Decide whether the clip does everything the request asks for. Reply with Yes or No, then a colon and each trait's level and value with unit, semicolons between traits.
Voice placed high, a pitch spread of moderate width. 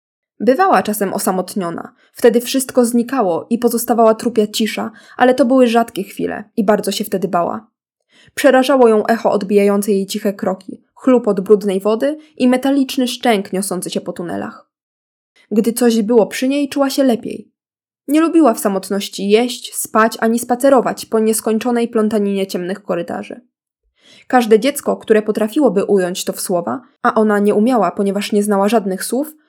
Yes: high, 225 Hz; average, 3.7 semitones